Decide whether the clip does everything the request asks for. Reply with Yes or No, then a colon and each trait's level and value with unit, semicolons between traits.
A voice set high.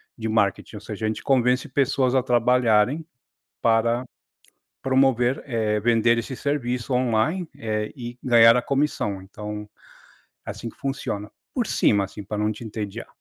No: low, 115 Hz